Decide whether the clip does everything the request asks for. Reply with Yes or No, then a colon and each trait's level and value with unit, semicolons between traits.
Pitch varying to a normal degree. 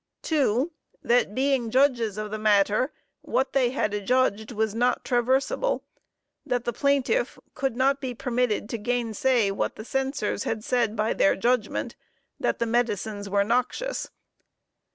Yes: average, 3.5 semitones